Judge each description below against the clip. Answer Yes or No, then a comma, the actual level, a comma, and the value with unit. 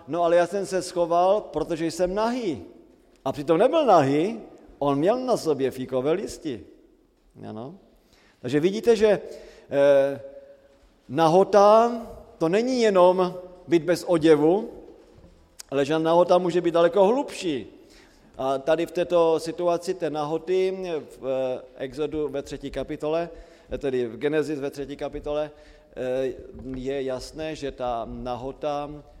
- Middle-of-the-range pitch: Yes, medium, 160 Hz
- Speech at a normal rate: Yes, average, 120 wpm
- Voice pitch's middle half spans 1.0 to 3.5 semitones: No, average, 4.4 semitones